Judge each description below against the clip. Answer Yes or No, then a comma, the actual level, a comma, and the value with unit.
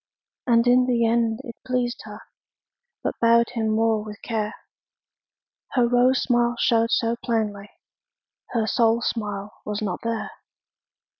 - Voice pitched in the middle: No, high, 230 Hz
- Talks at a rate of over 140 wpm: No, slow, 135 wpm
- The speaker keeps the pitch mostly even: Yes, narrow, 1.7 semitones